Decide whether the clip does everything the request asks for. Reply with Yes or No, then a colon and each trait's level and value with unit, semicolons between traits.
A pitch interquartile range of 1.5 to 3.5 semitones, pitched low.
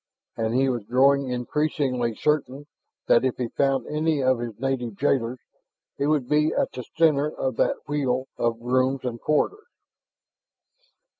Yes: average, 3.0 semitones; low, 130 Hz